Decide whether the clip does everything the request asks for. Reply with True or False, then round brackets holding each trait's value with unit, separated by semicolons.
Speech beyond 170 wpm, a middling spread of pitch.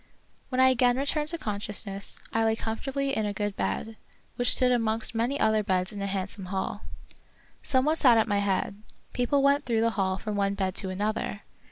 True (200 wpm; 4.0 semitones)